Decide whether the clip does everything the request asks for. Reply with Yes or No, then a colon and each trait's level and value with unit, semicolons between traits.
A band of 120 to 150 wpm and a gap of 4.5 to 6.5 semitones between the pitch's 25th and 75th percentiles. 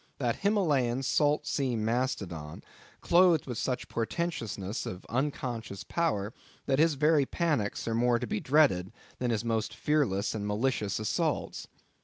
Yes: average, 140 wpm; wide, 5.6 semitones